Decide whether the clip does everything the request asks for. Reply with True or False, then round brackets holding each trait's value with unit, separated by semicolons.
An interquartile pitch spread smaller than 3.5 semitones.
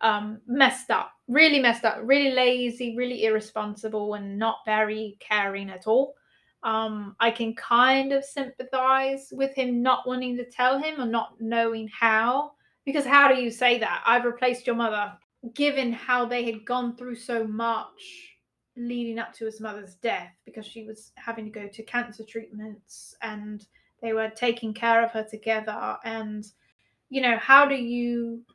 True (2.5 semitones)